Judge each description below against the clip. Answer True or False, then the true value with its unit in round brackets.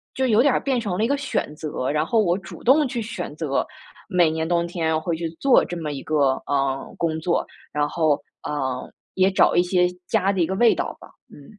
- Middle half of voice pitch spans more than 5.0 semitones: True (5.6 semitones)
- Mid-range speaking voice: True (170 Hz)